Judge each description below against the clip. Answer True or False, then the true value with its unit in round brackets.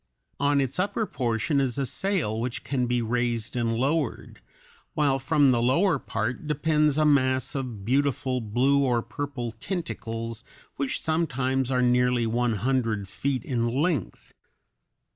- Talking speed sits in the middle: True (145 wpm)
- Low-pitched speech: True (130 Hz)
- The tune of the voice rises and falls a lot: False (3.3 semitones)